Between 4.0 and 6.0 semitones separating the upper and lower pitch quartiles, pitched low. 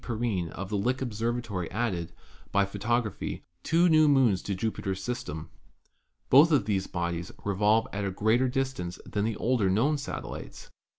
Yes: average, 4.4 semitones; low, 110 Hz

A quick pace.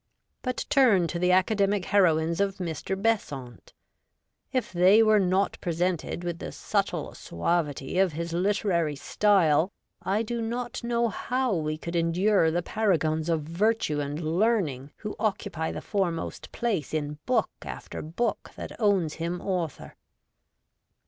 No: average, 140 wpm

